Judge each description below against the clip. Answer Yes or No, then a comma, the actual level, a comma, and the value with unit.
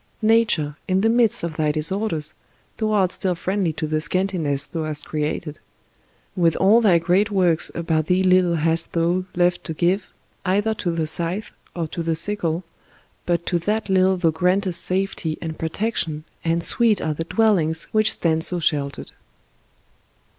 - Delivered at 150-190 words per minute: Yes, average, 165 wpm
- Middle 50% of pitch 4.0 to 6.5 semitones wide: No, average, 3.2 semitones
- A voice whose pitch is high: No, medium, 175 Hz